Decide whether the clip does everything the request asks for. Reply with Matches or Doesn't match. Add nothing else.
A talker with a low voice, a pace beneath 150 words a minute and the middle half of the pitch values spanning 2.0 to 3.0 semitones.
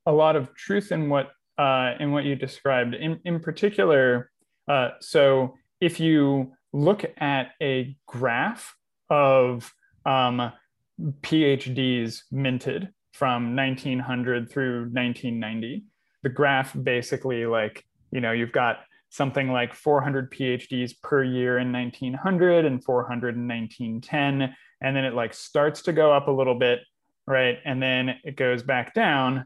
Matches